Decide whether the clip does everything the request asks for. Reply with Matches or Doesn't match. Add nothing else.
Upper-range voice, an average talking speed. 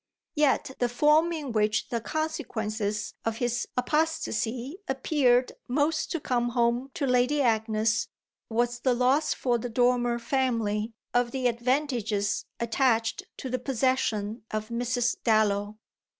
Doesn't match